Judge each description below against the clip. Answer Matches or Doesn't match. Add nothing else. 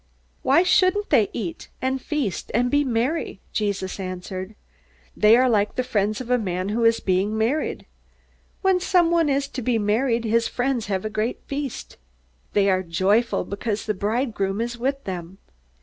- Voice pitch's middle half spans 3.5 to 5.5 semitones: Matches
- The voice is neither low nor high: Doesn't match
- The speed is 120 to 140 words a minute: Doesn't match